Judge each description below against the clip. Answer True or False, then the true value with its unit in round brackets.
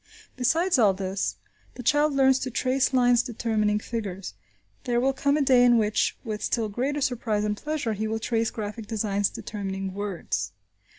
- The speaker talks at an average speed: True (170 wpm)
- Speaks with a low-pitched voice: False (225 Hz)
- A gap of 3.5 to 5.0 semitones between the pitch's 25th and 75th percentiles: True (3.8 semitones)